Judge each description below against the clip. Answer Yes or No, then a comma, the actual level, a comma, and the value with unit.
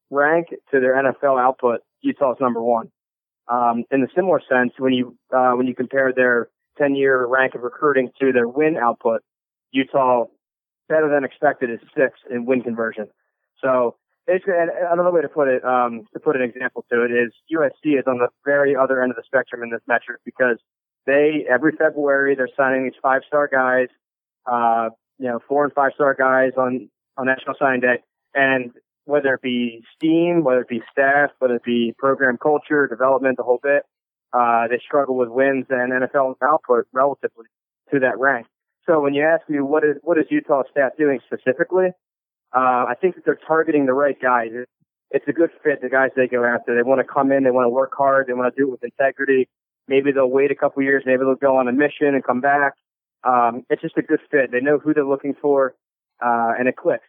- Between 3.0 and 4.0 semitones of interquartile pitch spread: No, narrow, 2.4 semitones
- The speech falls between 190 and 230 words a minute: Yes, fast, 205 wpm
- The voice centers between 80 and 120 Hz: No, low, 130 Hz